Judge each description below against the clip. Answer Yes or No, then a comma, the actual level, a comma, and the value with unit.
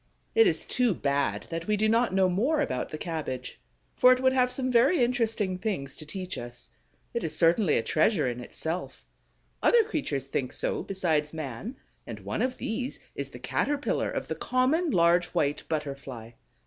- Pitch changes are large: Yes, wide, 8.9 semitones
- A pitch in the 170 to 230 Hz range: Yes, medium, 185 Hz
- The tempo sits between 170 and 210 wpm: Yes, average, 180 wpm